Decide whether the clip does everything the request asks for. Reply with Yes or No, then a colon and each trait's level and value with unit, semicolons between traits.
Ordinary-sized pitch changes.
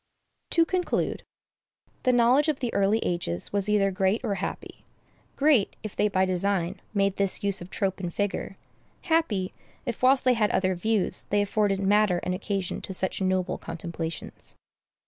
Yes: average, 3.0 semitones